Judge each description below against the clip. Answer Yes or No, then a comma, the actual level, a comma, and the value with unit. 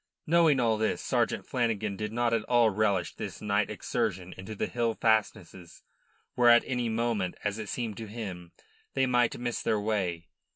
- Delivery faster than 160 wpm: Yes, average, 175 wpm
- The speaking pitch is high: No, low, 110 Hz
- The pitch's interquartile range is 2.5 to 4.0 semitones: Yes, average, 2.9 semitones